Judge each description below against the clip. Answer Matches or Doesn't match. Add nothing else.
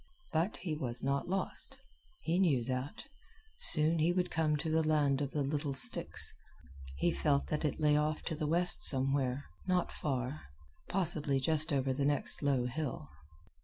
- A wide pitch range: Doesn't match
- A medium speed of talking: Matches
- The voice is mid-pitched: Matches